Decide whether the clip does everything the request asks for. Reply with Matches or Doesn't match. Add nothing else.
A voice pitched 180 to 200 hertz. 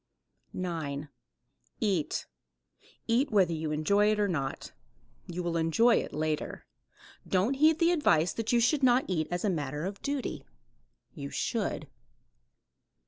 Matches